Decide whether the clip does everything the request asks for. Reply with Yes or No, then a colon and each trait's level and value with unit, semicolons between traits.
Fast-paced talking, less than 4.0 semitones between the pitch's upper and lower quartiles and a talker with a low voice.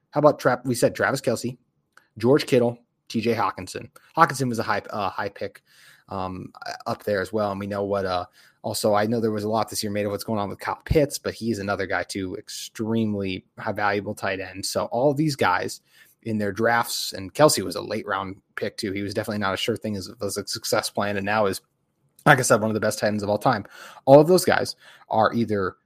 Yes: fast, 240 wpm; average, 2.7 semitones; low, 105 Hz